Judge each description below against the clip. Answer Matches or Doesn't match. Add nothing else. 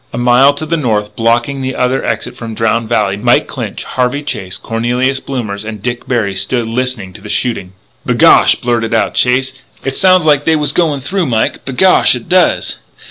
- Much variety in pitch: Doesn't match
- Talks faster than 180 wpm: Matches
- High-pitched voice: Doesn't match